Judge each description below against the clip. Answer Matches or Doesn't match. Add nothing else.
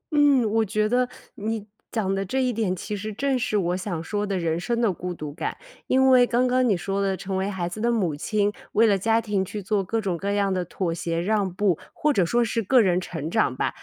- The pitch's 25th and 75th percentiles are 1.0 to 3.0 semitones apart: Doesn't match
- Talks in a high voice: Matches